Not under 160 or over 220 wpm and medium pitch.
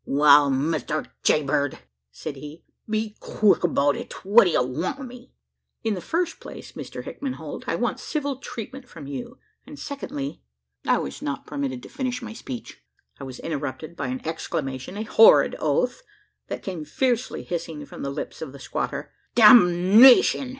Yes: average, 170 wpm; medium, 175 Hz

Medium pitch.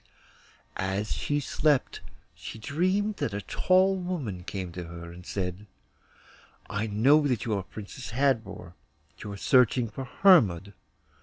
No: low, 110 Hz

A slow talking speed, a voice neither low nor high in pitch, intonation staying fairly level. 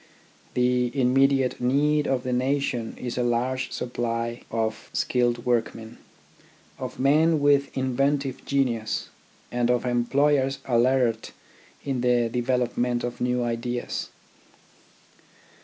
No: slow, 105 wpm; low, 125 Hz; narrow, 2.0 semitones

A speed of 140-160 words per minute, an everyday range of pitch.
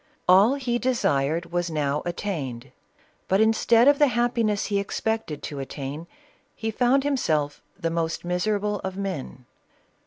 No: average, 145 wpm; wide, 6.4 semitones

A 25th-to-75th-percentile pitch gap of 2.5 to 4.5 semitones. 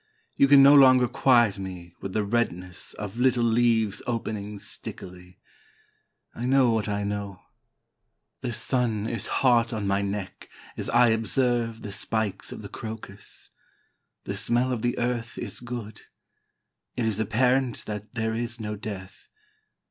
Yes: average, 3.0 semitones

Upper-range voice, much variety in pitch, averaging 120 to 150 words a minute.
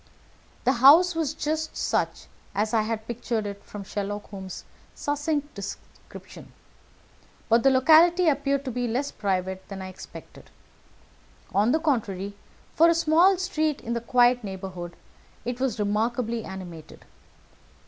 Yes: high, 235 Hz; wide, 6.4 semitones; average, 140 wpm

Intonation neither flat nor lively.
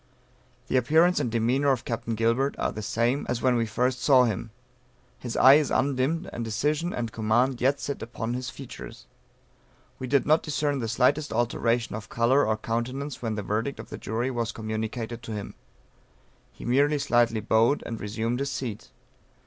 Yes: average, 3.3 semitones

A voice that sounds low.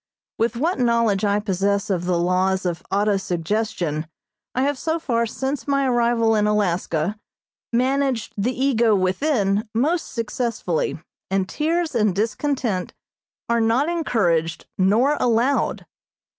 No: high, 225 Hz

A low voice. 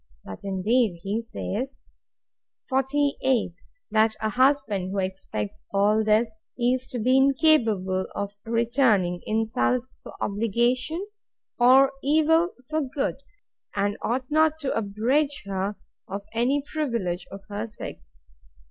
No: high, 230 Hz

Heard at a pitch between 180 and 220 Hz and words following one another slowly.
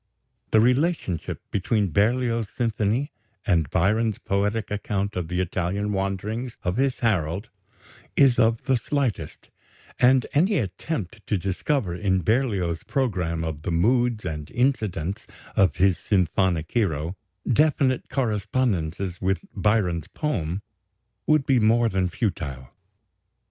No: low, 105 Hz; slow, 120 wpm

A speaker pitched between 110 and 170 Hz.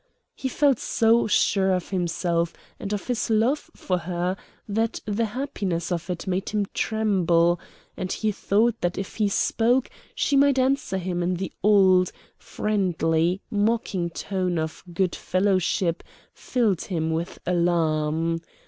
No: high, 190 Hz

